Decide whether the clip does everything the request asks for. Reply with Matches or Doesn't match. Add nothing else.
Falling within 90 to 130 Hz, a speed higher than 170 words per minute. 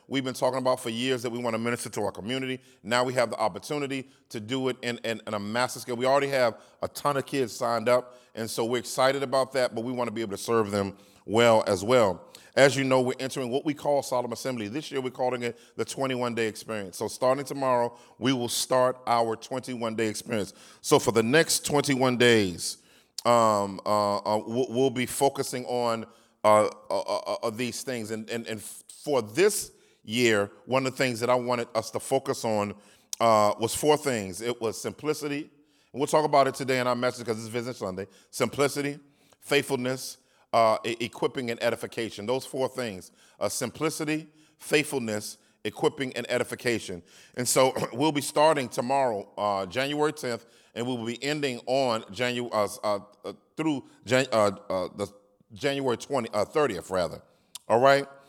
Matches